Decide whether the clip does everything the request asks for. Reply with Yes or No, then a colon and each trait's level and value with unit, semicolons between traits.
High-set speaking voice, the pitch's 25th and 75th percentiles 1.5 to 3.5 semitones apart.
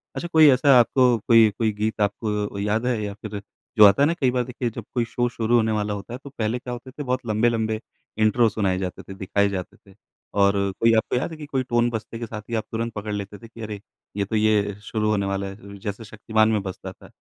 No: low, 110 Hz; average, 2.7 semitones